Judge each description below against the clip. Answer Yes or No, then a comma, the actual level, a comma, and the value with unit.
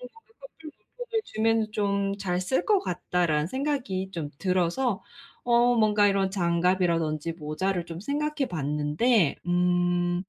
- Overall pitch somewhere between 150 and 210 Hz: Yes, high, 190 Hz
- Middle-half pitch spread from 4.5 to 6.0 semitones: Yes, wide, 5.5 semitones